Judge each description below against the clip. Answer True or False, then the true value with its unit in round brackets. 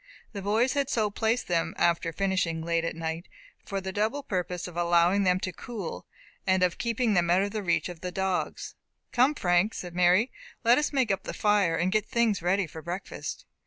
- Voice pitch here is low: False (190 Hz)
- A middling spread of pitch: True (3.7 semitones)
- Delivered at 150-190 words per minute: False (200 wpm)